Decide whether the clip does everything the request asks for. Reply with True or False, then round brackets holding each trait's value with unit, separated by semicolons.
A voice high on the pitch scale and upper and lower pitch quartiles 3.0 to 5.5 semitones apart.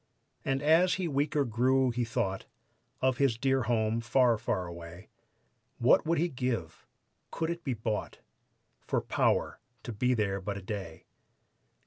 False (120 Hz; 4.4 semitones)